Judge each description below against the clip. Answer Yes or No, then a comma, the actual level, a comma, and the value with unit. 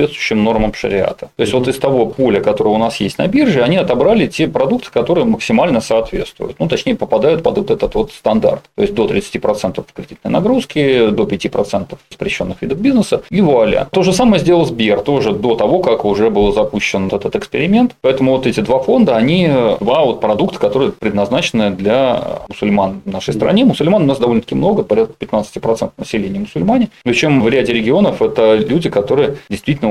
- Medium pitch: No, low, 130 Hz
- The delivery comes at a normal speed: No, fast, 185 wpm